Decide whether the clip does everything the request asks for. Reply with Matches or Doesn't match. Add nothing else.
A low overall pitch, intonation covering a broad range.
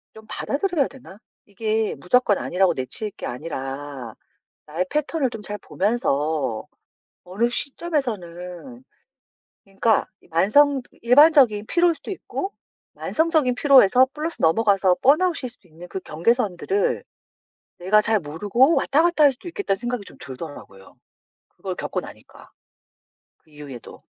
Doesn't match